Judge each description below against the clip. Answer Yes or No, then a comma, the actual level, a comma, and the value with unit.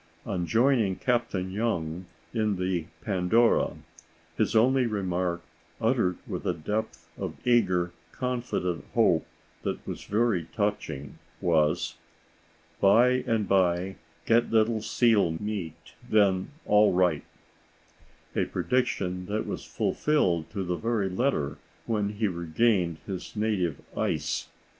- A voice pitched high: No, low, 100 Hz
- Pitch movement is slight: No, average, 4.2 semitones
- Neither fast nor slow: No, slow, 115 wpm